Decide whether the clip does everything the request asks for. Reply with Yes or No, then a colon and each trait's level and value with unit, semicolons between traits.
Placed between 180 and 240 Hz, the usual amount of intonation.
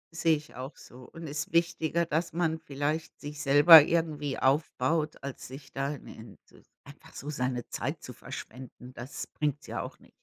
No: medium, 145 Hz; average, 3.2 semitones